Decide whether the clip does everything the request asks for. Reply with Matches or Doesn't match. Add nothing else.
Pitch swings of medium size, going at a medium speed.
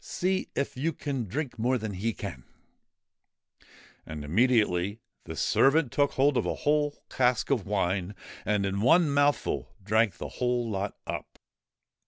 Doesn't match